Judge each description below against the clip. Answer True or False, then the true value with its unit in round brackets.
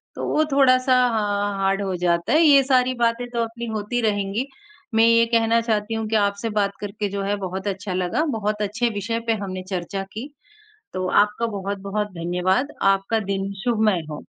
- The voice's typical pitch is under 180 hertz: False (210 Hz)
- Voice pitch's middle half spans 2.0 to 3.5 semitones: True (3.0 semitones)